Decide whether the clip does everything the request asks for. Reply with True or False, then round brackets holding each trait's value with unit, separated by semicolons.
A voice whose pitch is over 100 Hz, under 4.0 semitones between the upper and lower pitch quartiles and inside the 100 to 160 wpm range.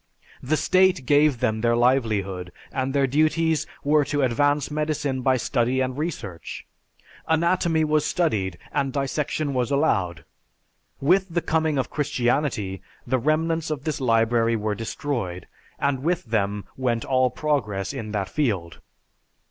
False (135 Hz; 5.0 semitones; 140 wpm)